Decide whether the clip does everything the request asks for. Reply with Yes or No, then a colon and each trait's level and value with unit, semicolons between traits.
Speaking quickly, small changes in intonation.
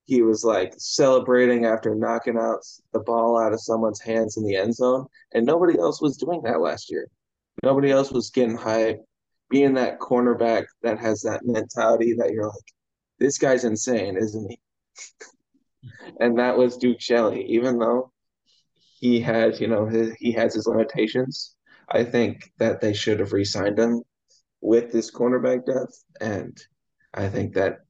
No: average, 165 wpm; narrow, 2.1 semitones